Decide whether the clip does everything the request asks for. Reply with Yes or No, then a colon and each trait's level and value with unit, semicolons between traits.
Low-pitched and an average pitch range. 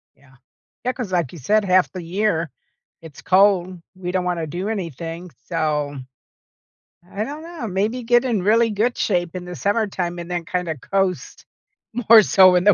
No: medium, 185 Hz; average, 3.6 semitones